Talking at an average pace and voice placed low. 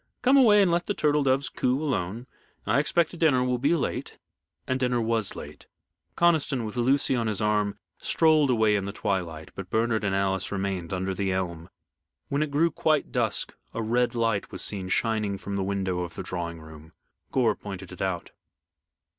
Yes: average, 190 wpm; low, 110 Hz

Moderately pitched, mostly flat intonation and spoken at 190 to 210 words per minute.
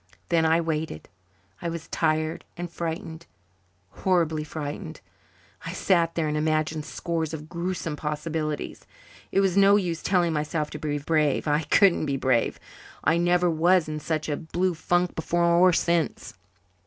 No: medium, 160 Hz; narrow, 2.0 semitones; average, 155 wpm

